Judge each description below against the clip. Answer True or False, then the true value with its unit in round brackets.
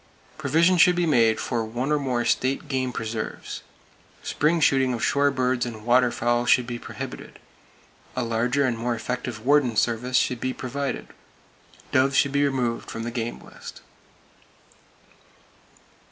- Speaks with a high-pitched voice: False (125 Hz)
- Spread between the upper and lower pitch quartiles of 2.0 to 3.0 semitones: True (2.7 semitones)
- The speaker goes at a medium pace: True (145 wpm)